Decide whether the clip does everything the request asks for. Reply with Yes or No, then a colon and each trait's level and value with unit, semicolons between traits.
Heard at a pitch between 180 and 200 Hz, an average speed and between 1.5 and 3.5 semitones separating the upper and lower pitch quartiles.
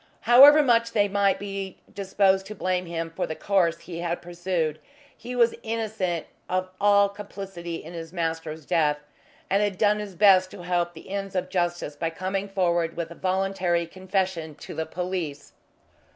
Yes: medium, 185 Hz; average, 170 wpm; average, 2.8 semitones